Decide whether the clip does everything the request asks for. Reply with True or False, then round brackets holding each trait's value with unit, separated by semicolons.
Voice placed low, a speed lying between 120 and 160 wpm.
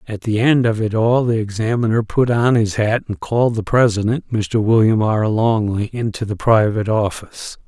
False (110 Hz; 190 wpm)